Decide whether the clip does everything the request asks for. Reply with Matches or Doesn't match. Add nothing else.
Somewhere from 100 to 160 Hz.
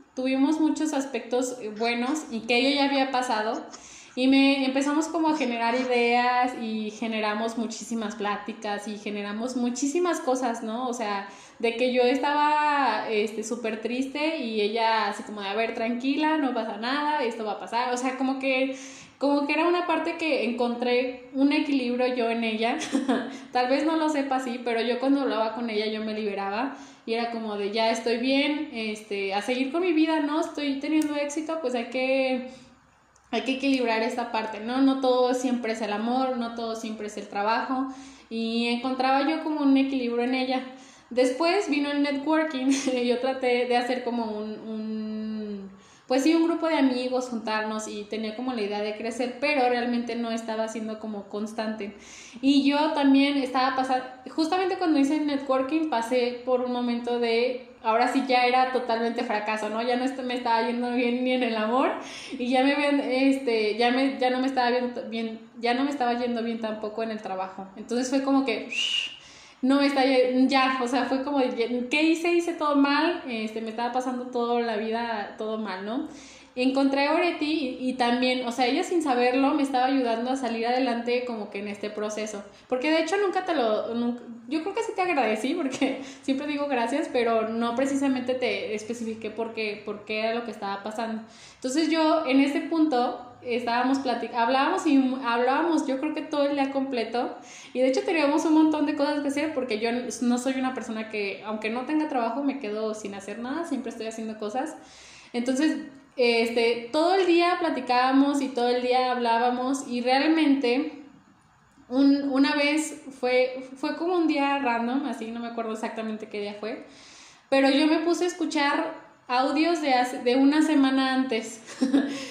Doesn't match